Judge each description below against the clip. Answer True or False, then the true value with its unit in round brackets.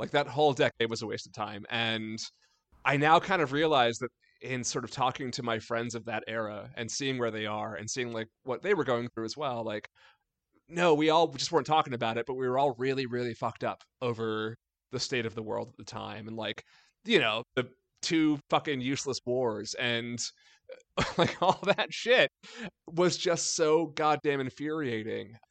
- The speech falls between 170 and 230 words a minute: True (200 wpm)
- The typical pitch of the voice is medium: False (125 Hz)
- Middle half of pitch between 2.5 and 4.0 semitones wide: False (4.8 semitones)